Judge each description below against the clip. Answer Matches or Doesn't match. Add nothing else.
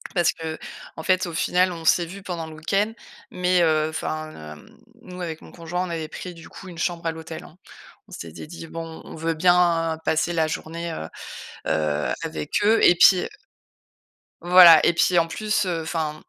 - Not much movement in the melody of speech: Matches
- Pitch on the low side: Doesn't match